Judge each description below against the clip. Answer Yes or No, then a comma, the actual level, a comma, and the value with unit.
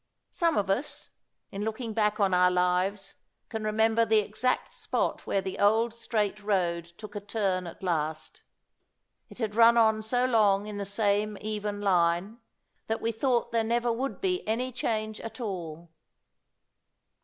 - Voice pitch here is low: No, high, 210 Hz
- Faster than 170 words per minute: No, average, 160 wpm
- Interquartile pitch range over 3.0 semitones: No, average, 2.7 semitones